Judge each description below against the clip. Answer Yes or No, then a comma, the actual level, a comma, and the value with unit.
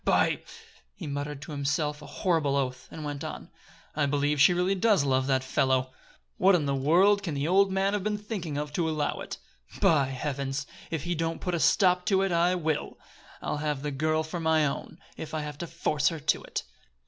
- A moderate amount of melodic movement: Yes, average, 3.8 semitones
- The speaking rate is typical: No, fast, 220 wpm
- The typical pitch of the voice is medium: Yes, medium, 155 Hz